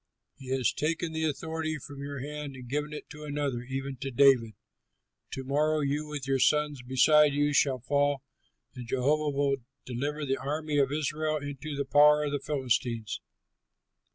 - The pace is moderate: Yes, average, 170 wpm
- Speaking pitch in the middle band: Yes, medium, 145 Hz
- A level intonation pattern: Yes, narrow, 2.1 semitones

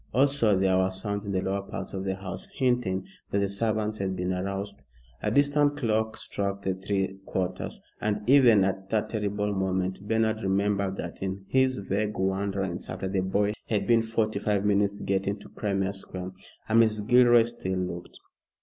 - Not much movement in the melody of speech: Yes, narrow, 2.3 semitones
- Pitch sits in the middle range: No, low, 100 Hz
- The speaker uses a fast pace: No, average, 180 wpm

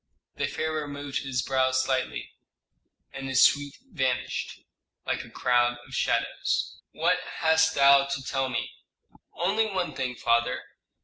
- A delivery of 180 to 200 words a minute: No, slow, 135 wpm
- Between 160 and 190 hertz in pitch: No, low, 135 Hz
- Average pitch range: No, narrow, 2.0 semitones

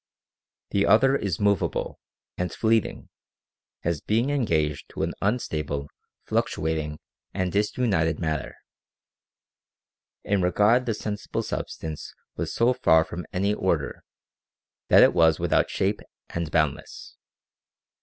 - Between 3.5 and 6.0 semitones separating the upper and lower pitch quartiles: Yes, average, 4.9 semitones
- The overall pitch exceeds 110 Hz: No, very low, 90 Hz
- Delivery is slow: Yes, slow, 115 wpm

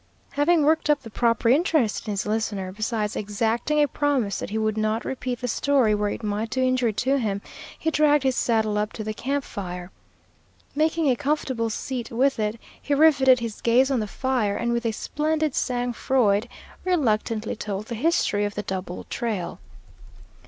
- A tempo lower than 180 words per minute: No, average, 185 wpm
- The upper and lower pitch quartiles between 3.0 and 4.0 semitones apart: No, average, 4.4 semitones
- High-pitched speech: Yes, high, 235 Hz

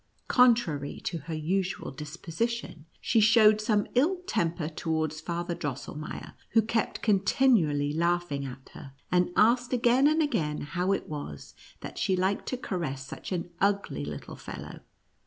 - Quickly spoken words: No, average, 150 wpm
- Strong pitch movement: Yes, wide, 6.7 semitones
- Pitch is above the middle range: No, medium, 175 Hz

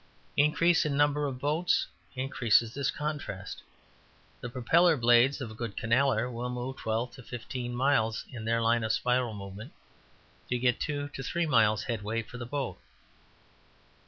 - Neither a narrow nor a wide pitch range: Yes, average, 3.6 semitones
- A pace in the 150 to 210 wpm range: Yes, average, 160 wpm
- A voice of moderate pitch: No, low, 125 Hz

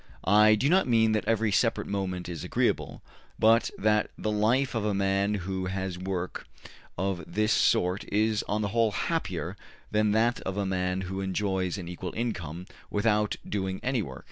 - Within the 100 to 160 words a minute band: No, average, 175 wpm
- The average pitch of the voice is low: Yes, low, 100 Hz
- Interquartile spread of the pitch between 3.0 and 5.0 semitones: No, narrow, 2.5 semitones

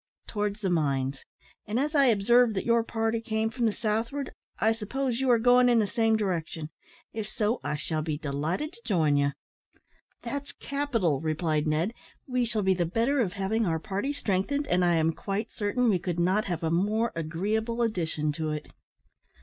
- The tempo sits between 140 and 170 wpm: No, average, 190 wpm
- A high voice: Yes, high, 210 Hz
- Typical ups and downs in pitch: No, wide, 6.0 semitones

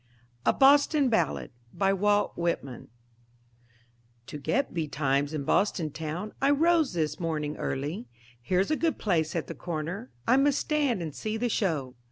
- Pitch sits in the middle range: Yes, medium, 180 Hz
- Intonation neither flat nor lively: No, wide, 8.3 semitones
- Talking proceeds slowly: No, average, 155 wpm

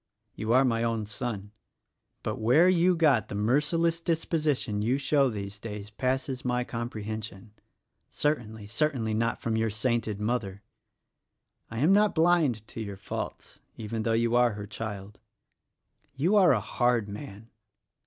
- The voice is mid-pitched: No, low, 115 Hz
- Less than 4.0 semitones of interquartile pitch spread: No, average, 4.6 semitones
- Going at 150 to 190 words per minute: Yes, average, 155 wpm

